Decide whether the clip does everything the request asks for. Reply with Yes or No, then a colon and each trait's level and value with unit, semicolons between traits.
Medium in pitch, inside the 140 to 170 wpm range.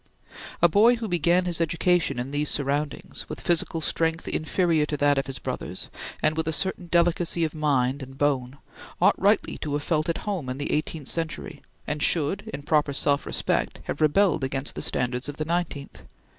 No: medium, 155 Hz; average, 190 wpm